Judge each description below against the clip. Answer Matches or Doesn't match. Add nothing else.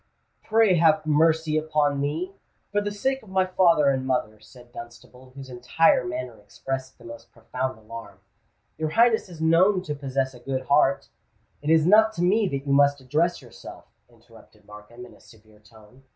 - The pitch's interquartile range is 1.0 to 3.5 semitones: Doesn't match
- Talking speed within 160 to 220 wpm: Matches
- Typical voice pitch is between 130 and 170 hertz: Matches